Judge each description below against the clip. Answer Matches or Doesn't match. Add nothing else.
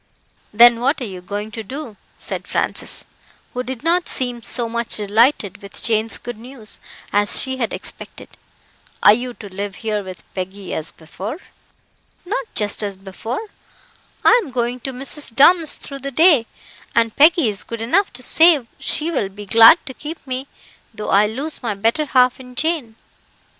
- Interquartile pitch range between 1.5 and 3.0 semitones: Doesn't match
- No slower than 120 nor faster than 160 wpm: Doesn't match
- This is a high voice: Matches